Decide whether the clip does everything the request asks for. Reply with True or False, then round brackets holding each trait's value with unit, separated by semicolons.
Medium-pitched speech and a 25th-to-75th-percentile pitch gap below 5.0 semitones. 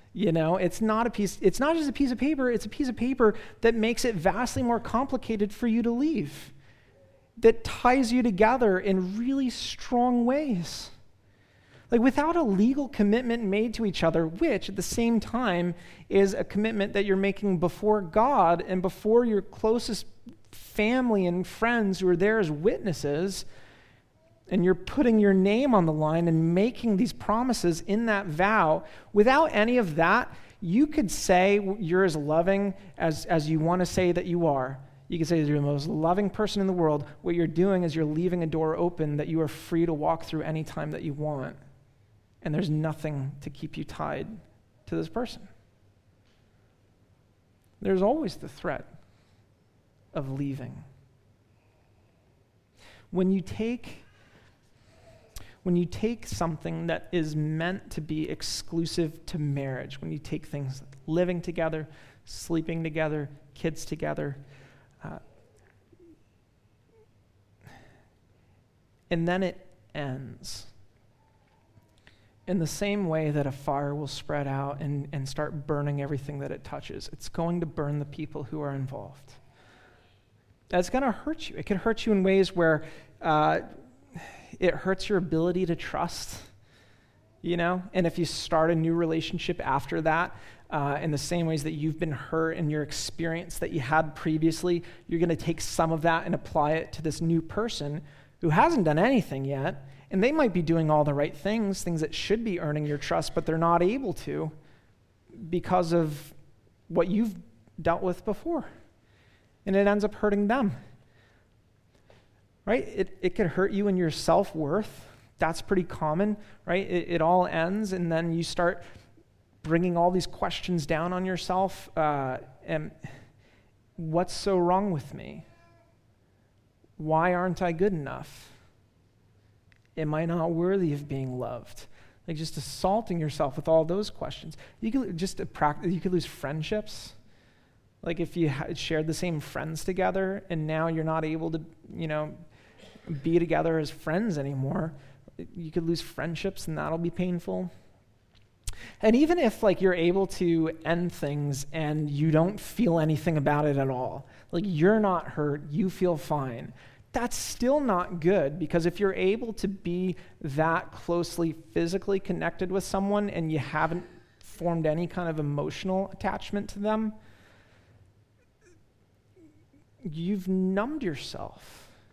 False (165 Hz; 5.6 semitones)